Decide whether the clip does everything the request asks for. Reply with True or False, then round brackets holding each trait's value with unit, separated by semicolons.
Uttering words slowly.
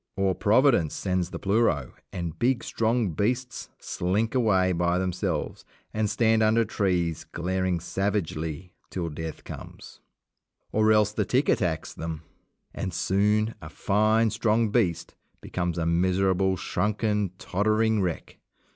True (130 wpm)